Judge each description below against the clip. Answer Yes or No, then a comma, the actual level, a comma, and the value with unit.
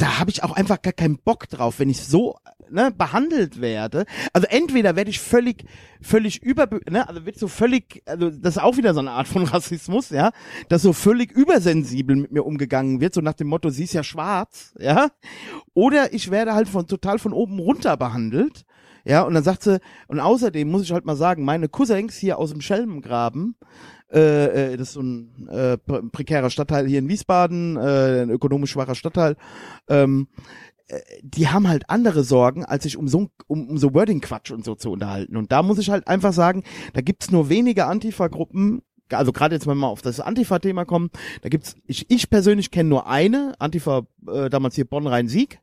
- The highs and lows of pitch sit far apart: Yes, wide, 6.8 semitones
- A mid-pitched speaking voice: Yes, medium, 170 Hz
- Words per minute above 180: Yes, fast, 190 wpm